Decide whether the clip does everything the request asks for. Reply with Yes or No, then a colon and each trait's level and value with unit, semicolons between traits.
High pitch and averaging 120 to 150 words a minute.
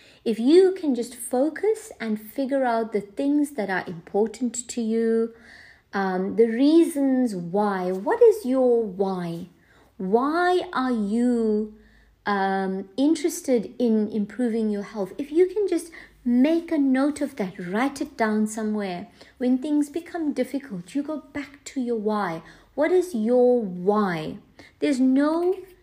Yes: high, 245 Hz; average, 140 wpm